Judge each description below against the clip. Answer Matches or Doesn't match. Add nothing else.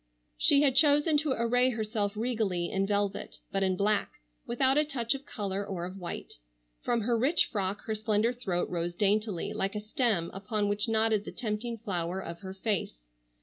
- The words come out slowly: Doesn't match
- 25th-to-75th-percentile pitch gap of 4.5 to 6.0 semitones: Doesn't match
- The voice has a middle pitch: Doesn't match